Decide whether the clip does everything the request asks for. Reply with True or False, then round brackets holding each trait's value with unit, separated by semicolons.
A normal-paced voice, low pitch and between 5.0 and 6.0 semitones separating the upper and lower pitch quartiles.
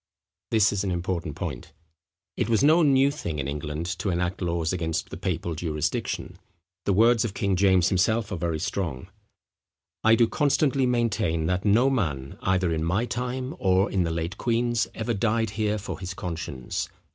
True (175 wpm; 95 Hz; 5.4 semitones)